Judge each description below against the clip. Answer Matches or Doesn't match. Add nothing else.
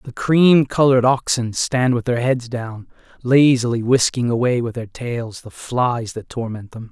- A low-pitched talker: Matches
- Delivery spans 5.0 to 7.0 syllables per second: Doesn't match